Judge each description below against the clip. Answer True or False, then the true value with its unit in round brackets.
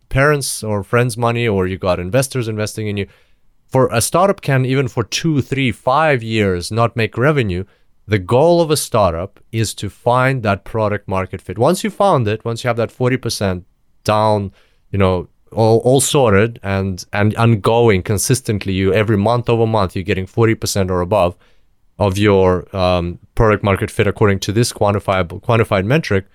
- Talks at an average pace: True (175 wpm)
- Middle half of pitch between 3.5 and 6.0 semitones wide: True (3.8 semitones)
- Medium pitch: False (110 Hz)